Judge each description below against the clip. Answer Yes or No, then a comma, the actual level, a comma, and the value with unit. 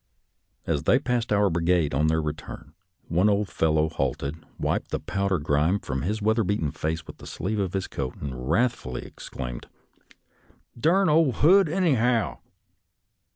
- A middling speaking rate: Yes, average, 160 wpm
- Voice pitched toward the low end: Yes, very low, 90 Hz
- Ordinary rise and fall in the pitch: No, wide, 7.1 semitones